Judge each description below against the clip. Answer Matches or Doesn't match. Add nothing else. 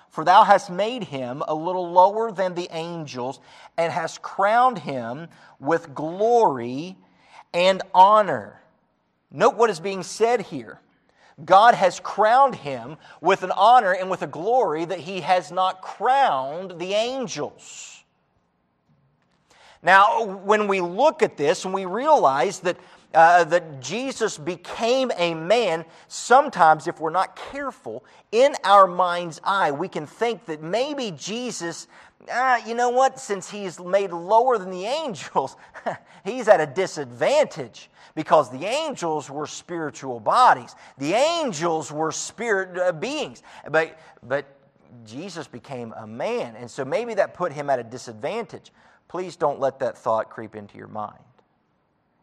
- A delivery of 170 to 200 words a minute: Doesn't match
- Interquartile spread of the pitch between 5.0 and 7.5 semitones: Matches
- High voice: Doesn't match